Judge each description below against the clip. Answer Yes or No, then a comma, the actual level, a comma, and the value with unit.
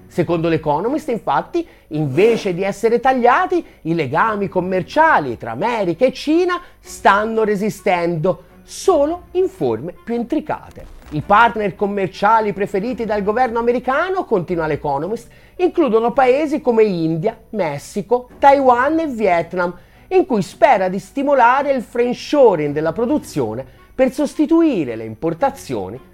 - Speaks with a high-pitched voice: Yes, high, 225 Hz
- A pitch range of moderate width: No, wide, 7.5 semitones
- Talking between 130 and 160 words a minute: No, slow, 115 wpm